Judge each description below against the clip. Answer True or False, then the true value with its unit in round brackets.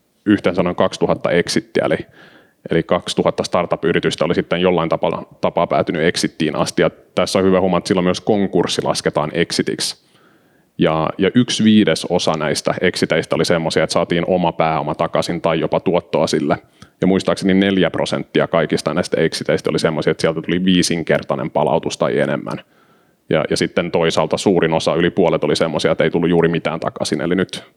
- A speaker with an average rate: False (160 wpm)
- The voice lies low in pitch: True (85 Hz)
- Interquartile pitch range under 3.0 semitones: True (2.4 semitones)